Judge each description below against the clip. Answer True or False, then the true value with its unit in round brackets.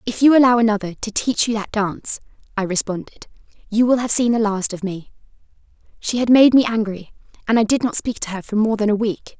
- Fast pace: True (230 wpm)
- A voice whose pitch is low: False (220 Hz)